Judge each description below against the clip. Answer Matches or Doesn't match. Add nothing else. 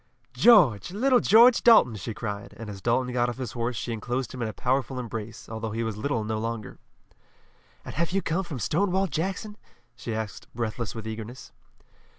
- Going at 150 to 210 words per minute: Matches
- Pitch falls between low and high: Doesn't match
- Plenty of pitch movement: Matches